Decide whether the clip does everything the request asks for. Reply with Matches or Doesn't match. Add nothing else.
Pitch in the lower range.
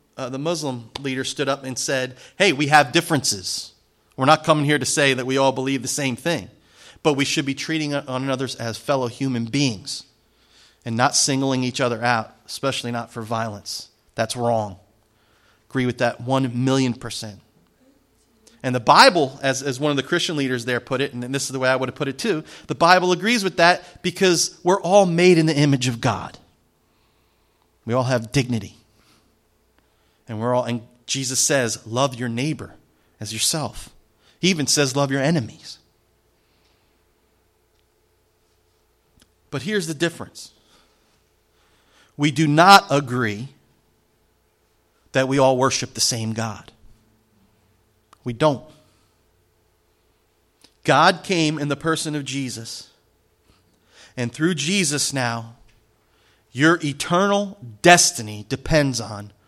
Matches